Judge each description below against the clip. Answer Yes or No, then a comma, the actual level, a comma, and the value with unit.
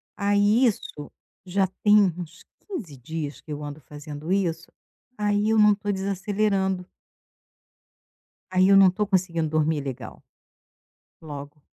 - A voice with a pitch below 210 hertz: Yes, medium, 185 Hz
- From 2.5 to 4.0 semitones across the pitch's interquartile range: No, average, 4.7 semitones